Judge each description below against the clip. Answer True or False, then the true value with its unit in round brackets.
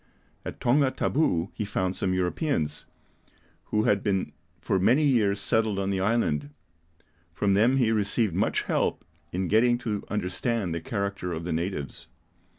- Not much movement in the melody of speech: False (4.0 semitones)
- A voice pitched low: True (100 Hz)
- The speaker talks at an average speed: True (155 wpm)